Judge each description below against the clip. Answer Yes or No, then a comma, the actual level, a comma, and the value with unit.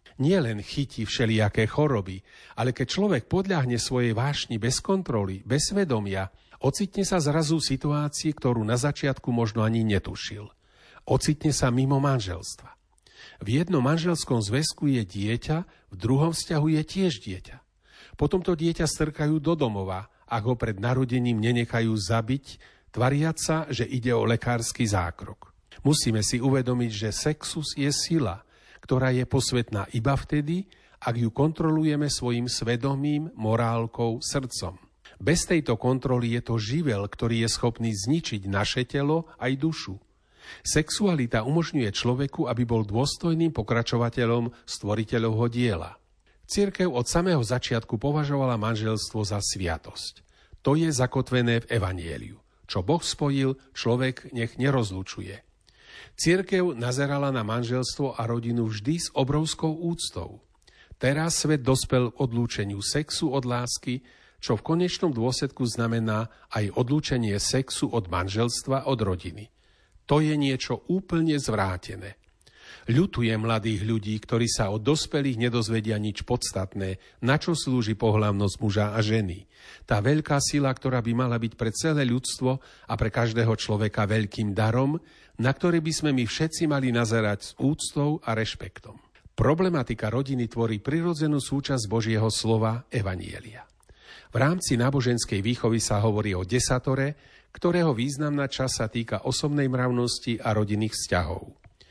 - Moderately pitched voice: No, low, 125 Hz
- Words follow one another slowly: No, average, 135 wpm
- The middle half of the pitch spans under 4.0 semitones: No, average, 4.6 semitones